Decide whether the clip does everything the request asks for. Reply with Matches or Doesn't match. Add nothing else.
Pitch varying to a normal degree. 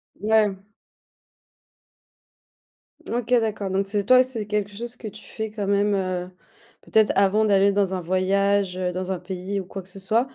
Doesn't match